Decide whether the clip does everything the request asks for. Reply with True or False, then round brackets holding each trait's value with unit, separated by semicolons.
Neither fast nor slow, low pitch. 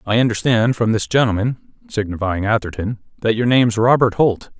True (145 wpm; 115 Hz)